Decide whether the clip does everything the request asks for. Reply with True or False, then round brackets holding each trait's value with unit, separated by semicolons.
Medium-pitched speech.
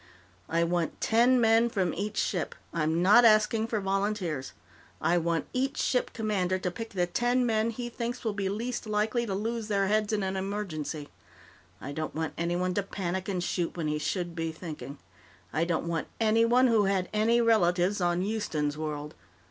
False (195 Hz)